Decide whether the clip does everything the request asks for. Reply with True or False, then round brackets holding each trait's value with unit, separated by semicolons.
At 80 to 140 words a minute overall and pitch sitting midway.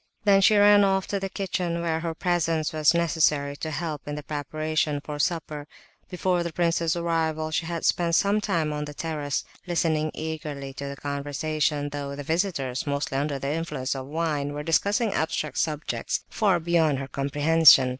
False (175 wpm; 155 Hz)